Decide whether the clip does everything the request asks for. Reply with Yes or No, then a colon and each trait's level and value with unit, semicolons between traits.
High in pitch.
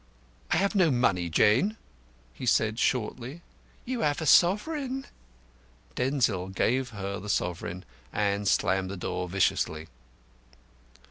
No: low, 110 Hz